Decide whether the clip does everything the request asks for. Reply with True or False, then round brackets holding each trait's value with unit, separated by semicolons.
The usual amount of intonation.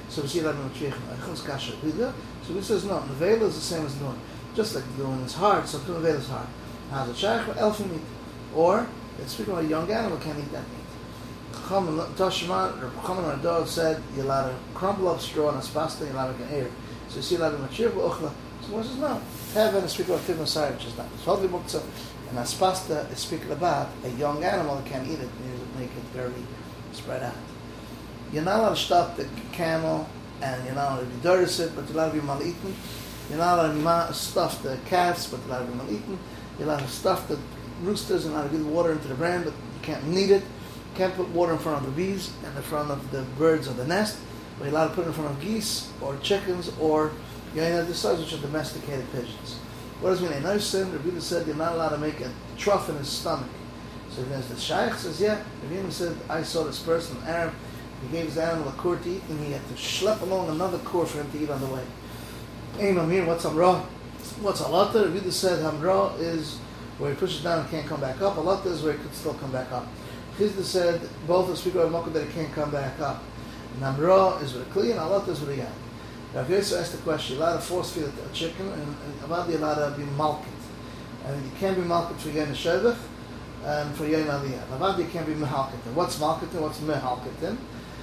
True (4.4 semitones)